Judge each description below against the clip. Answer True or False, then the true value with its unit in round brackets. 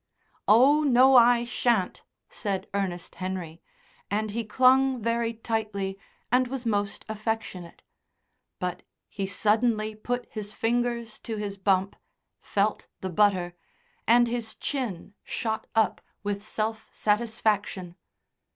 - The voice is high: True (215 Hz)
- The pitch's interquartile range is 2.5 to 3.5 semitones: True (3.1 semitones)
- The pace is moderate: False (115 wpm)